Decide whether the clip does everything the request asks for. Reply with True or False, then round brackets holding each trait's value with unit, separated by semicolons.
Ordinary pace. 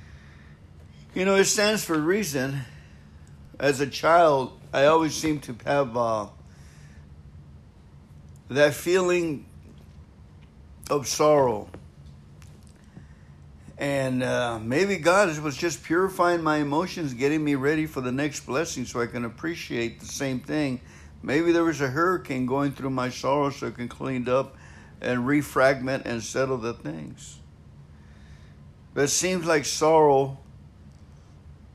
False (130 wpm)